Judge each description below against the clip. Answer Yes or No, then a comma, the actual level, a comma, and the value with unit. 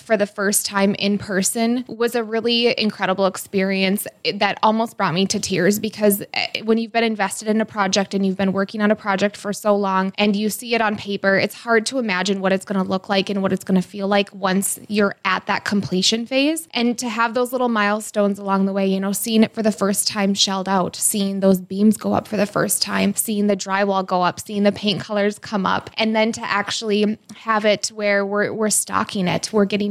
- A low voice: No, high, 205 Hz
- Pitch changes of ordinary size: No, narrow, 1.9 semitones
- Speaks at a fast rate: Yes, fast, 235 wpm